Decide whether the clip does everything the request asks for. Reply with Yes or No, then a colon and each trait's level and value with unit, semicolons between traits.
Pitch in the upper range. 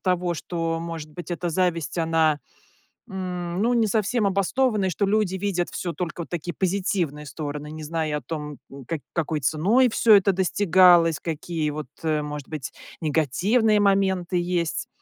No: medium, 175 Hz